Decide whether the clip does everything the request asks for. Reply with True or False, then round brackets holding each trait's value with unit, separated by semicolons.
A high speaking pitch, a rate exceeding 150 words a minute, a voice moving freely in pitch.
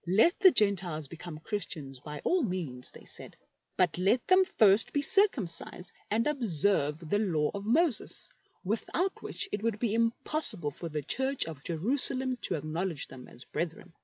True (195 Hz; 160 wpm; 7.3 semitones)